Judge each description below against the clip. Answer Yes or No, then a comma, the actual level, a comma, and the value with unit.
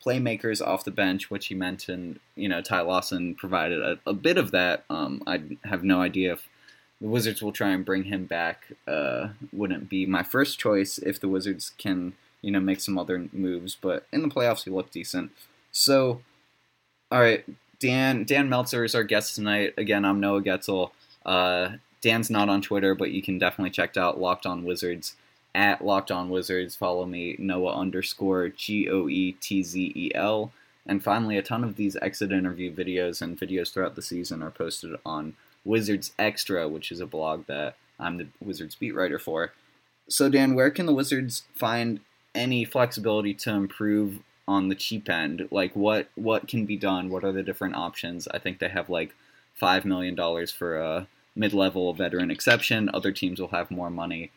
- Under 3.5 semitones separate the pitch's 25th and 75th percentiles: Yes, average, 2.8 semitones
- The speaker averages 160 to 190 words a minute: Yes, average, 180 wpm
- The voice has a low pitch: Yes, very low, 95 Hz